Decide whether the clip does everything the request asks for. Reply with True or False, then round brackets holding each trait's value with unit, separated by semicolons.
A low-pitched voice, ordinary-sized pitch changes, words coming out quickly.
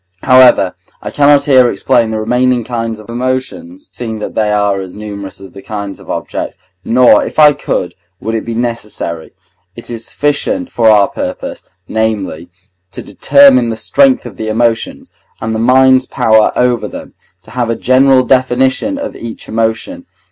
False (120 Hz; 3.2 semitones; 170 wpm)